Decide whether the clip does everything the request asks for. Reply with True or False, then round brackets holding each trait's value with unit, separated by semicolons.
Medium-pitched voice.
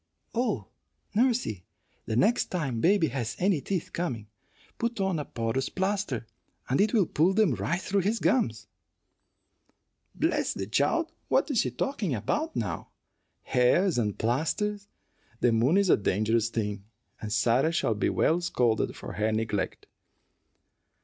True (145 Hz)